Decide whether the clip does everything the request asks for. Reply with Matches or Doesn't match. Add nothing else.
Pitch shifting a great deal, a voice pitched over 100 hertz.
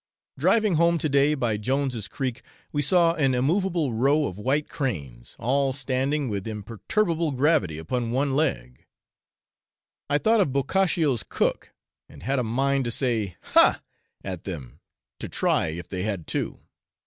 Matches